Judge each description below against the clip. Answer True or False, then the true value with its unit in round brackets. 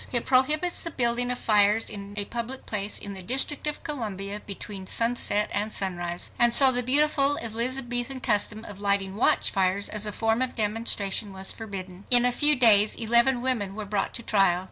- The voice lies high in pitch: True (225 Hz)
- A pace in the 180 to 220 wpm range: True (185 wpm)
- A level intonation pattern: False (3.7 semitones)